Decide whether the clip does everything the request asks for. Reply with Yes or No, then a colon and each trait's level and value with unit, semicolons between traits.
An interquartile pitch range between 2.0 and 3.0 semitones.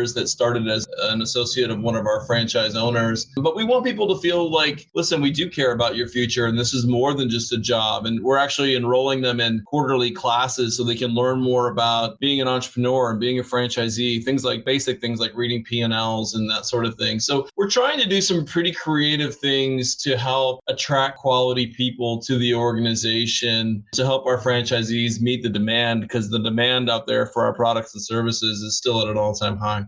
Yes: narrow, 2.4 semitones